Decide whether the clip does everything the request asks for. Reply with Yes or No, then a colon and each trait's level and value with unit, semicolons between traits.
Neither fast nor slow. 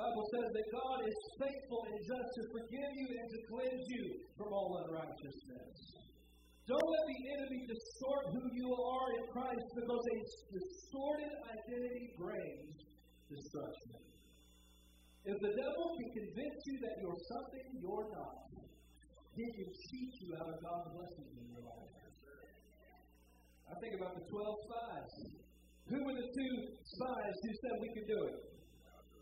Yes: average, 150 wpm